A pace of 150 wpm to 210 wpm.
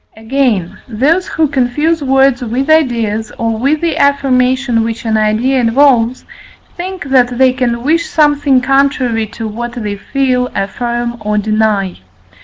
No: average, 140 wpm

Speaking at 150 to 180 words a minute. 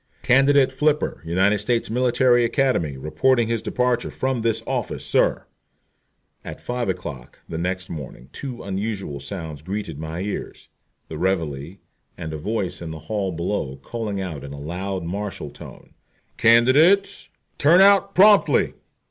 No: average, 140 wpm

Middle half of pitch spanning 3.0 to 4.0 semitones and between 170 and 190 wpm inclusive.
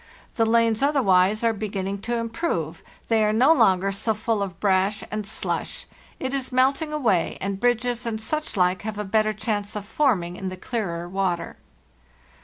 Yes: average, 3.5 semitones; average, 180 wpm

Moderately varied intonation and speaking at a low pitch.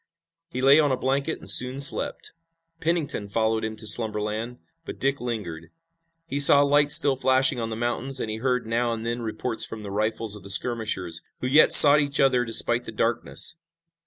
Yes: average, 3.7 semitones; low, 120 Hz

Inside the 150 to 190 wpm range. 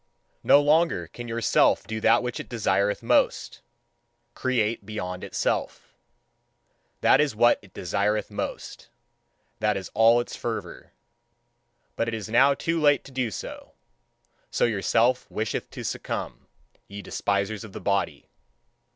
No: average, 140 wpm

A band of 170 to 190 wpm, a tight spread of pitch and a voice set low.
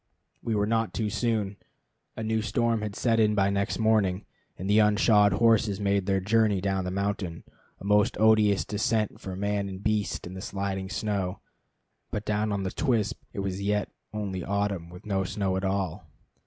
Yes: average, 185 wpm; narrow, 1.8 semitones; low, 100 Hz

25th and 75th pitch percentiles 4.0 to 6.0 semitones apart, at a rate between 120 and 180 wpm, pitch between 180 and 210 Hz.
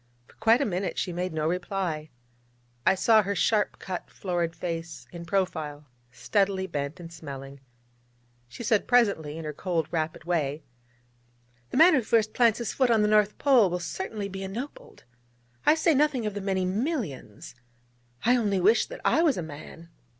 Yes: average, 5.1 semitones; average, 175 wpm; high, 190 Hz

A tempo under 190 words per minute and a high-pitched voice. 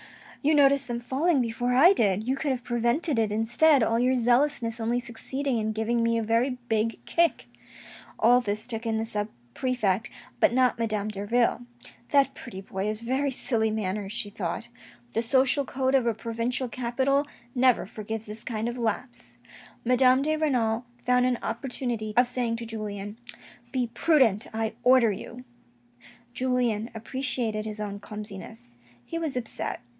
Yes: average, 170 wpm; high, 235 Hz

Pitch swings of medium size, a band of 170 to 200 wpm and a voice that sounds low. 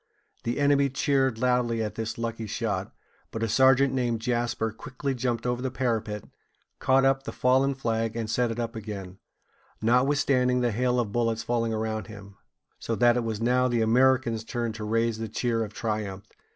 No: narrow, 2.2 semitones; average, 180 wpm; low, 115 Hz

